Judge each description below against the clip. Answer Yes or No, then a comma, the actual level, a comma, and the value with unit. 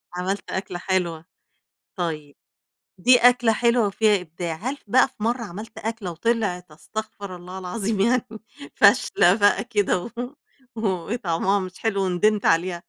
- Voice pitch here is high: Yes, high, 200 Hz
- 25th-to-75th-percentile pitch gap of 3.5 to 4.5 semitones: Yes, average, 3.9 semitones